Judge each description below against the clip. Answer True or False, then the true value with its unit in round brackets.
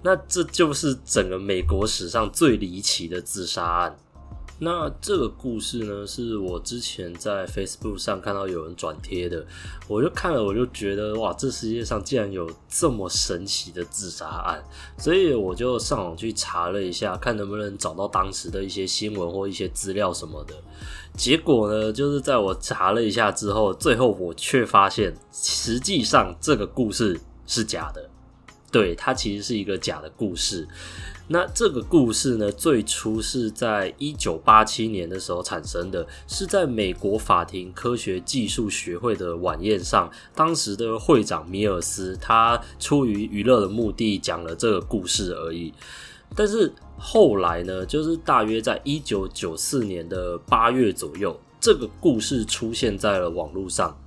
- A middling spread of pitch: True (4.2 semitones)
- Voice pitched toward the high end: False (100 Hz)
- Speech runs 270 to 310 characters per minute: False (255 characters per minute)